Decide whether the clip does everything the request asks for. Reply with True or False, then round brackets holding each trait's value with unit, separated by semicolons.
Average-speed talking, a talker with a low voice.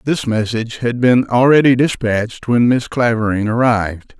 True (145 wpm; 120 Hz)